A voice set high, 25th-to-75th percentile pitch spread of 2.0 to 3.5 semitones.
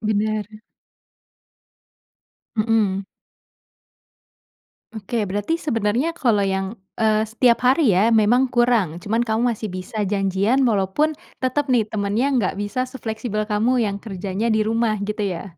Yes: high, 215 Hz; average, 2.9 semitones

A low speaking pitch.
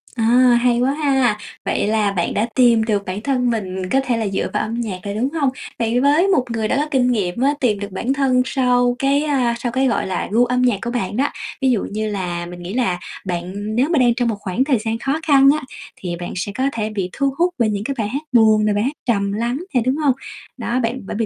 No: high, 235 Hz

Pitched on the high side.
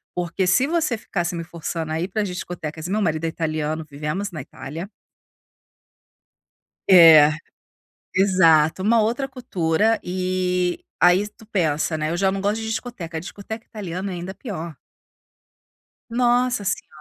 No: medium, 180 Hz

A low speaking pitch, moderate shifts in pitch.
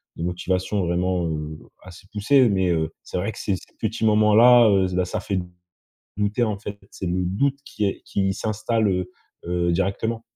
Yes: low, 100 Hz; average, 3.2 semitones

